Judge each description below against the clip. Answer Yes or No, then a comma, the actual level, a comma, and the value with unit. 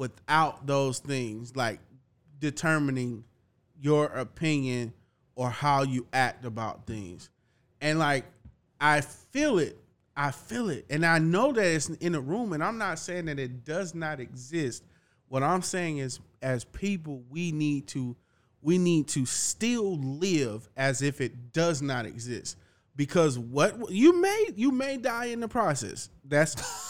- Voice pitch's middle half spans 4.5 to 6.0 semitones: Yes, average, 4.8 semitones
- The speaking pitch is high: No, medium, 140 Hz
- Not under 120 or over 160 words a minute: Yes, average, 155 wpm